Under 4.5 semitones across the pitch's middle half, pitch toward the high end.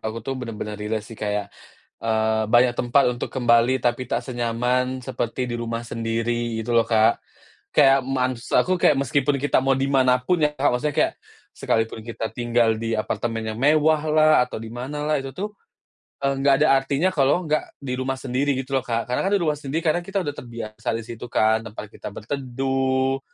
No: average, 3.1 semitones; low, 125 Hz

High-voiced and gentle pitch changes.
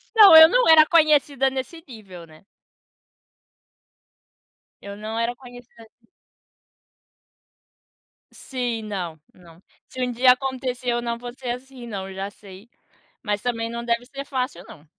No: high, 240 Hz; average, 3.7 semitones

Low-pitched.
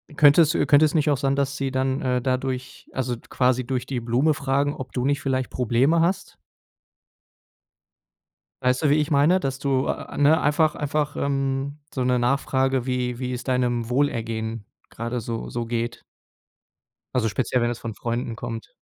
Yes: low, 130 Hz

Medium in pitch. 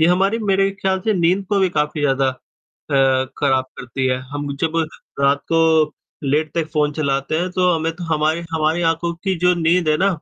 Yes: medium, 160 Hz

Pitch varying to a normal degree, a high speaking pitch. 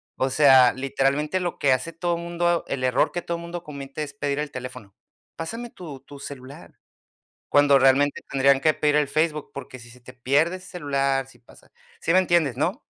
No: average, 3.9 semitones; medium, 145 Hz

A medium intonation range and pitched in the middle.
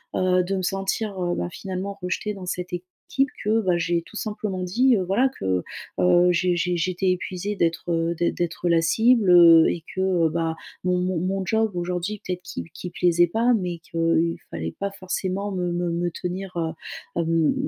No: narrow, 2.2 semitones; medium, 180 Hz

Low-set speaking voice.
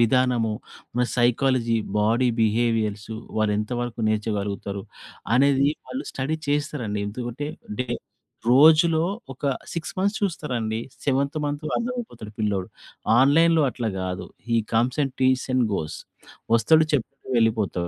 Yes: low, 125 Hz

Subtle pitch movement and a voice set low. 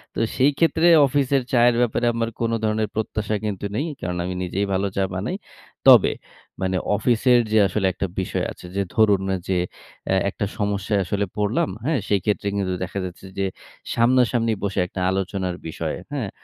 No: average, 3.6 semitones; low, 105 Hz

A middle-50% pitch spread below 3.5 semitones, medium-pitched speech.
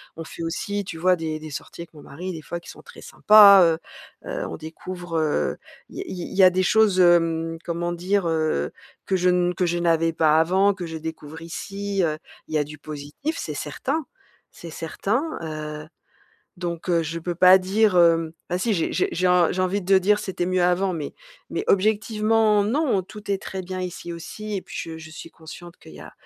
Yes: average, 3.1 semitones; medium, 180 Hz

